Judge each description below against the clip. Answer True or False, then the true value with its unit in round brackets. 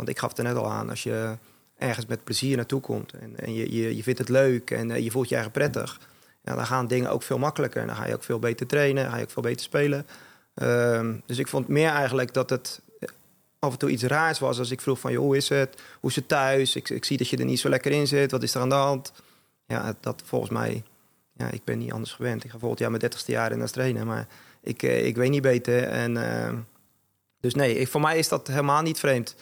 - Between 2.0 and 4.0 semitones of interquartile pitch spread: True (2.8 semitones)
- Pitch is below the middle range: True (130 Hz)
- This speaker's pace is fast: True (265 wpm)